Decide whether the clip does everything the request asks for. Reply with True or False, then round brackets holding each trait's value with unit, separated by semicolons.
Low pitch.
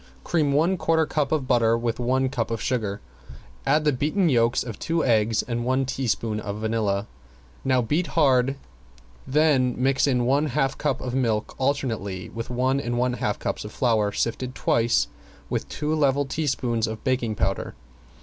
True (125 Hz)